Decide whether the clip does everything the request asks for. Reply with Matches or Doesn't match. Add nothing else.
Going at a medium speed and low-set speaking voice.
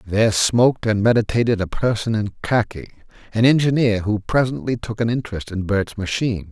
Matches